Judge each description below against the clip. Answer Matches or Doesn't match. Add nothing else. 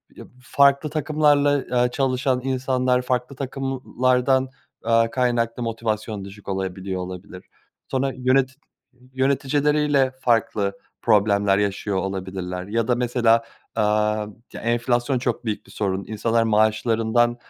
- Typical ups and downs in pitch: Matches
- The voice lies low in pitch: Matches